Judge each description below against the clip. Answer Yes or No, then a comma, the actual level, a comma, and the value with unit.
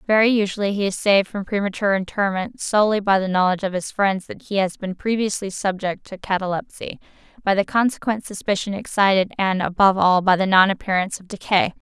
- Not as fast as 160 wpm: No, average, 185 wpm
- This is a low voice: No, high, 195 Hz